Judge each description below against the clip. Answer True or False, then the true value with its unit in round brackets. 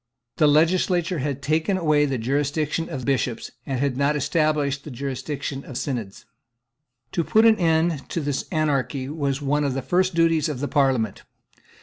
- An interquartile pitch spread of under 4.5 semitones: True (2.9 semitones)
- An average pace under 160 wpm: False (165 wpm)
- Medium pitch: True (145 Hz)